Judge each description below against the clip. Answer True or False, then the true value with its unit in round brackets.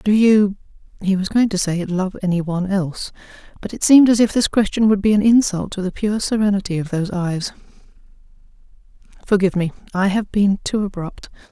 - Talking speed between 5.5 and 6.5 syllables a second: True (5.9 syllables/s)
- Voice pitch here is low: False (195 Hz)